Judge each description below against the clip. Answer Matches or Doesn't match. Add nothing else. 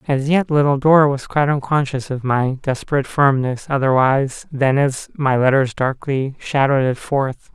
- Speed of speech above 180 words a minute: Doesn't match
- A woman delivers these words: Doesn't match